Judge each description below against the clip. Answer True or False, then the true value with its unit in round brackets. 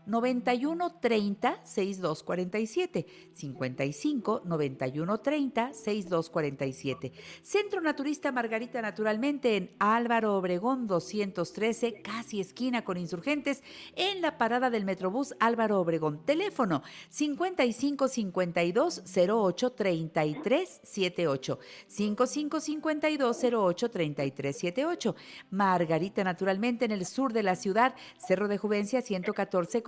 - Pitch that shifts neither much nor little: False (5.9 semitones)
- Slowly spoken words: True (70 wpm)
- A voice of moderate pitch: False (215 Hz)